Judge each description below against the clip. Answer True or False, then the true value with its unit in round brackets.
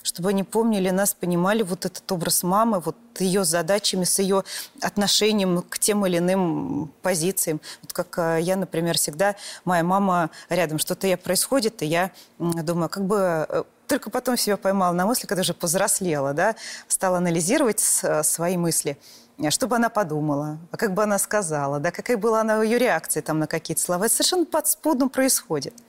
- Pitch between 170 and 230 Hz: True (185 Hz)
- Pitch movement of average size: True (3.8 semitones)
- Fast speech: True (165 wpm)